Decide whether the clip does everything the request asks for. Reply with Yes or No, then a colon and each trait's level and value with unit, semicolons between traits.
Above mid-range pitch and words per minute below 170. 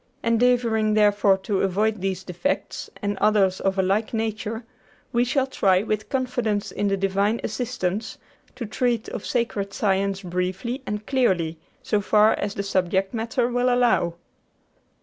Yes: high, 210 Hz; average, 150 wpm